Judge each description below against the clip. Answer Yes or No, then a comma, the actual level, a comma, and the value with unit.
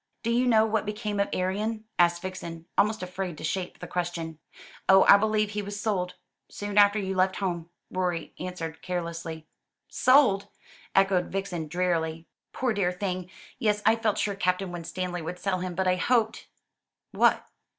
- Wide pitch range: No, average, 2.8 semitones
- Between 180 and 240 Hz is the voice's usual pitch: Yes, medium, 185 Hz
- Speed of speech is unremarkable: Yes, average, 170 wpm